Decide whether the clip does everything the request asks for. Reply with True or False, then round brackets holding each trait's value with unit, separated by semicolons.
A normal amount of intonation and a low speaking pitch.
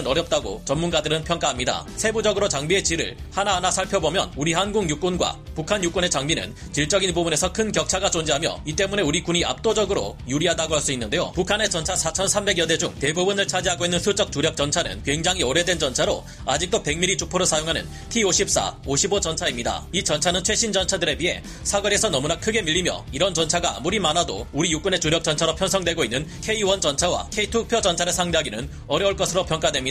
False (3.6 semitones; 180 Hz)